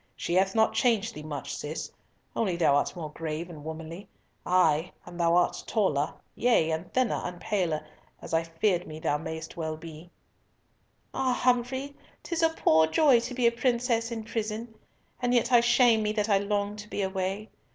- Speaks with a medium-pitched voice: No, high, 195 Hz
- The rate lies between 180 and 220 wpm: Yes, average, 185 wpm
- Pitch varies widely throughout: Yes, wide, 6.3 semitones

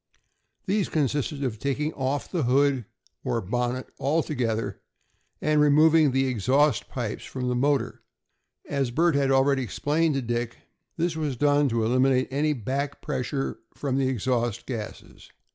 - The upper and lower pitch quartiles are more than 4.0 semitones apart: No, average, 3.0 semitones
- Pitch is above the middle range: No, low, 135 Hz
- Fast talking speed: No, average, 145 wpm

